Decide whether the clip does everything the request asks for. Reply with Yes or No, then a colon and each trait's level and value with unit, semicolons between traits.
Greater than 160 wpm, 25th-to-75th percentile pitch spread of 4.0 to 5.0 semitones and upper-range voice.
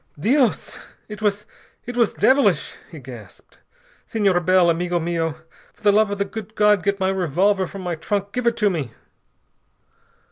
No: average, 170 wpm; average, 3.1 semitones; high, 200 Hz